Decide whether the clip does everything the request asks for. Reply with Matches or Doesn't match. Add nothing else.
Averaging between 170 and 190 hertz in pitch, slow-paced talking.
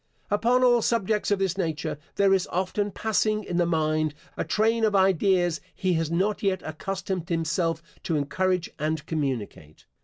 Doesn't match